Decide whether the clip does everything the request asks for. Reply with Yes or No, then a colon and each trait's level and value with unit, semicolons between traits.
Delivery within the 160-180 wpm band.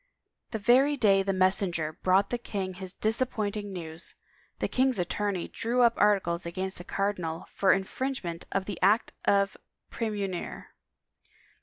No: average, 140 wpm